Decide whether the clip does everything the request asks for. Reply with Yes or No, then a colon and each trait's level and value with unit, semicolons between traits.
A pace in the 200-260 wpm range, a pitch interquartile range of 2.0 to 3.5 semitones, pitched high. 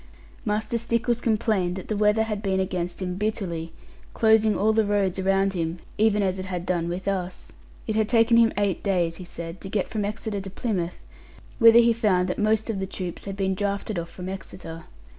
Yes: fast, 205 wpm; average, 3.1 semitones; high, 195 Hz